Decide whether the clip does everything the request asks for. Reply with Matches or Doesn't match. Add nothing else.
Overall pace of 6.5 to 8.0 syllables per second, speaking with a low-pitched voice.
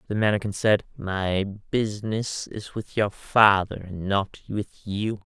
Doesn't match